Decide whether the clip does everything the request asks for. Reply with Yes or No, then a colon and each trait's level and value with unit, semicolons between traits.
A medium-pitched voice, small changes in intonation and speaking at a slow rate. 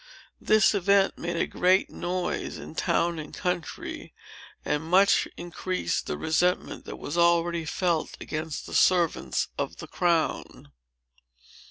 Yes: medium, 175 Hz; narrow, 2.1 semitones; slow, 130 wpm